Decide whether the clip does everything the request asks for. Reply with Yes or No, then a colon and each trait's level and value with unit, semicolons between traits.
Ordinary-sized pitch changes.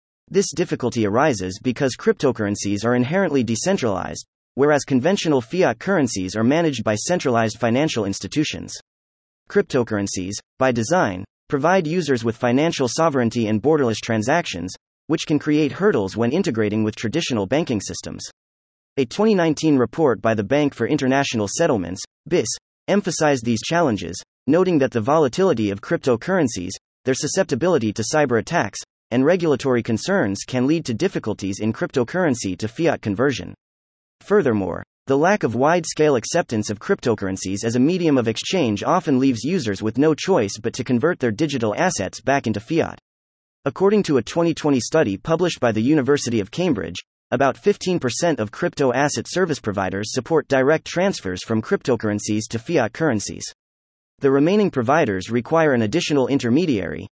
No: wide, 6.7 semitones